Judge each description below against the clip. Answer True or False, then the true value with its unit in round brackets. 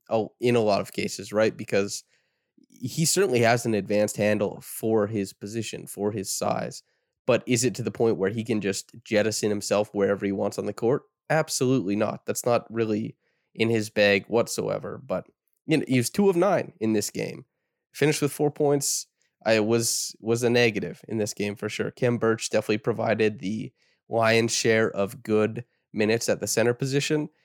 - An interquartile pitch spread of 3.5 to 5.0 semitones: False (2.9 semitones)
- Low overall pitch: True (110 Hz)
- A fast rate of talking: False (190 wpm)